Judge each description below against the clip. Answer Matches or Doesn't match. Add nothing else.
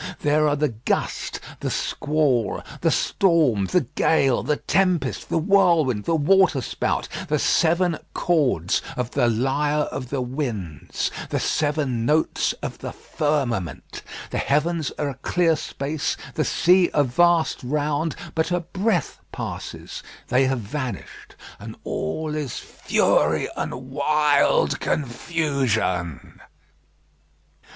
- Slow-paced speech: Matches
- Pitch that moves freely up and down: Doesn't match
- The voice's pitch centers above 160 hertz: Doesn't match